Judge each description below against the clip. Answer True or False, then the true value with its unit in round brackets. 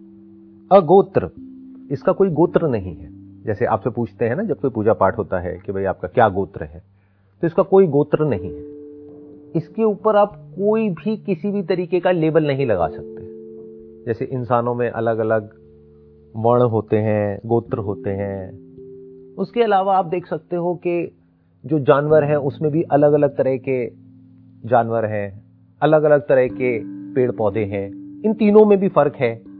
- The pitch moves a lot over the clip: True (7.7 semitones)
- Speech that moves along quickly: False (170 wpm)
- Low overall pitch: True (130 Hz)